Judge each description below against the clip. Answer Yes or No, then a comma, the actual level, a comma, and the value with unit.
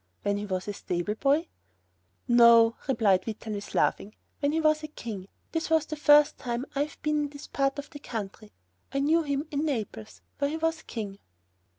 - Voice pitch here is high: Yes, very high, 275 Hz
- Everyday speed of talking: Yes, average, 195 wpm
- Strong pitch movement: Yes, wide, 6.1 semitones